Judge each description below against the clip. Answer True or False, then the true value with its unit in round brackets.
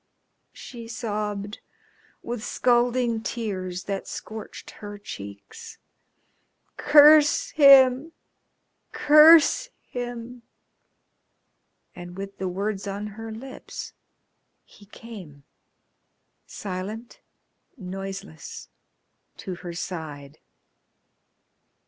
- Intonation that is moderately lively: True (4.4 semitones)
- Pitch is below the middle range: False (215 Hz)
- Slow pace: True (75 wpm)